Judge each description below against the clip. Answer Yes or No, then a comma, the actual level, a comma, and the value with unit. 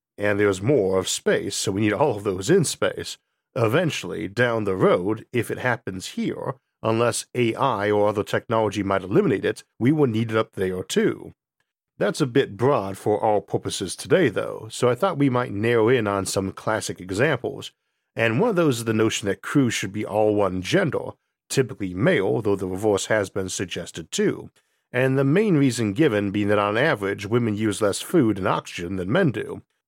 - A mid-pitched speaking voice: No, low, 110 Hz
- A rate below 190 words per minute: No, average, 195 wpm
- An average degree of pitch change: Yes, average, 3.6 semitones